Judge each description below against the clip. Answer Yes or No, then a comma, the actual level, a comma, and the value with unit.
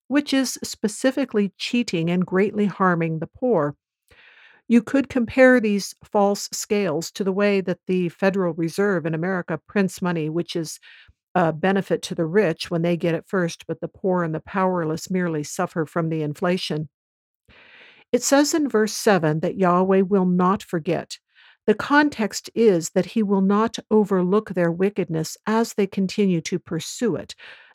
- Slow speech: No, average, 160 wpm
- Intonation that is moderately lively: Yes, average, 3.9 semitones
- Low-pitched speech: No, high, 190 Hz